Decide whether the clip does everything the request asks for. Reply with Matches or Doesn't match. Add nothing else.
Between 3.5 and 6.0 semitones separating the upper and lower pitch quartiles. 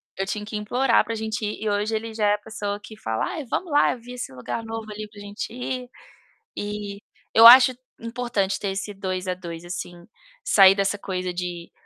Doesn't match